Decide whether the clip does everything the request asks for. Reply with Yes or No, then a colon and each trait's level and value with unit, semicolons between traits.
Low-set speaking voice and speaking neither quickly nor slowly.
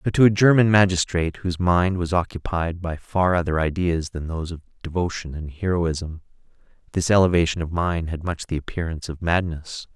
Yes: very low, 85 Hz; average, 175 wpm